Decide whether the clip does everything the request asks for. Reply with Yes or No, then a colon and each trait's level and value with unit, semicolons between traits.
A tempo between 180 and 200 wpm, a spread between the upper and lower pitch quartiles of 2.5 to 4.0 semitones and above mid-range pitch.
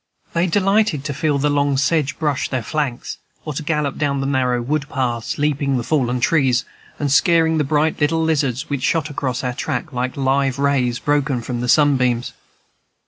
No: average, 185 wpm; average, 2.9 semitones; medium, 140 Hz